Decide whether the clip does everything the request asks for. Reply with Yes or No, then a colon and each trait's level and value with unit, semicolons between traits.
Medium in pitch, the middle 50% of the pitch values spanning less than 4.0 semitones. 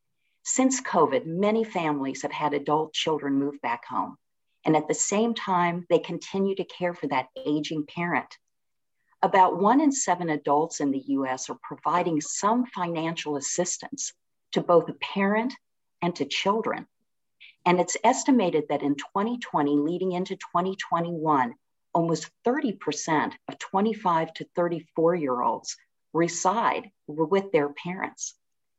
No: medium, 175 Hz; average, 4.5 semitones